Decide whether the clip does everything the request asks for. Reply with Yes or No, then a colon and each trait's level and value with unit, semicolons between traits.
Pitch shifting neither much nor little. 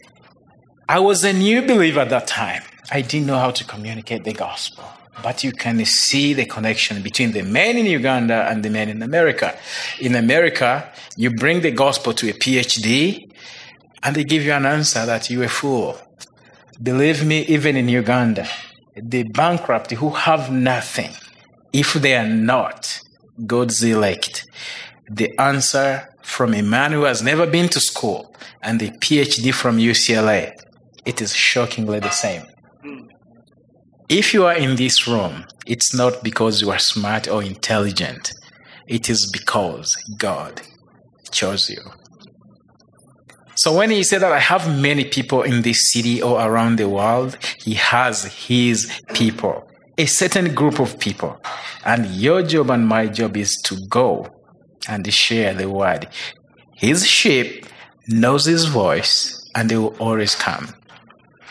Yes: average, 4.1 semitones